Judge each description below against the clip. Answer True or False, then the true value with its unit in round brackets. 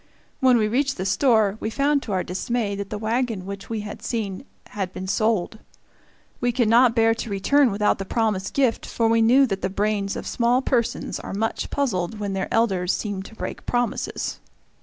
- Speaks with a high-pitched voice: True (220 Hz)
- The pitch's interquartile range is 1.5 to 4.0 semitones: True (3.4 semitones)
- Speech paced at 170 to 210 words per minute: True (200 wpm)